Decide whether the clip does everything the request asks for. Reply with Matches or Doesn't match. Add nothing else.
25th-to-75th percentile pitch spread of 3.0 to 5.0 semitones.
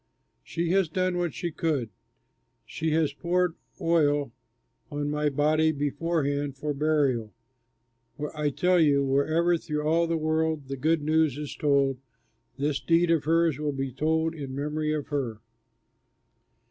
Doesn't match